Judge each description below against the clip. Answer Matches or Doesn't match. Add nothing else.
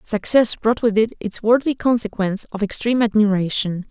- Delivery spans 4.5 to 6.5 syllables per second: Matches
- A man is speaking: Doesn't match